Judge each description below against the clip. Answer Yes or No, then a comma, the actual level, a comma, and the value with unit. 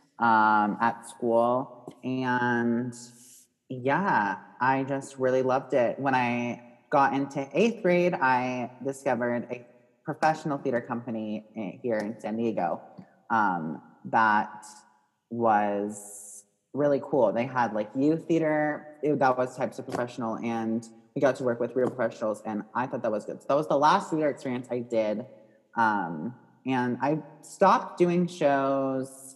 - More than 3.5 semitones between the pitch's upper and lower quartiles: No, average, 3.1 semitones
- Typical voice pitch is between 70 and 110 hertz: No, low, 125 Hz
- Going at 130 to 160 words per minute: Yes, average, 145 wpm